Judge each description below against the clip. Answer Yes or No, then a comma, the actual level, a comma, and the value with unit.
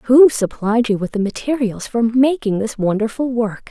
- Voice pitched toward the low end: No, high, 230 Hz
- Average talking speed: Yes, average, 180 wpm